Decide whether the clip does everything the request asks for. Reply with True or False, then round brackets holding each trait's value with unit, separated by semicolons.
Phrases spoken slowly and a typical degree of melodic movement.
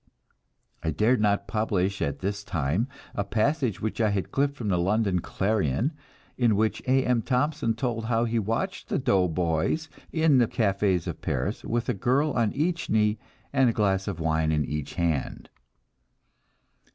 False (165 wpm; 4.7 semitones)